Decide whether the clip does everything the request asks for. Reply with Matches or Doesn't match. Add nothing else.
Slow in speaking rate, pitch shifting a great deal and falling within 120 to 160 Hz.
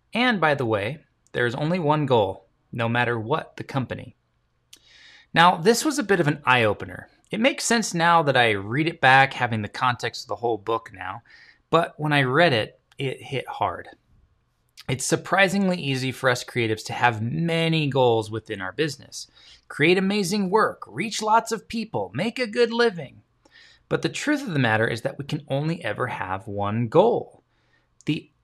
Doesn't match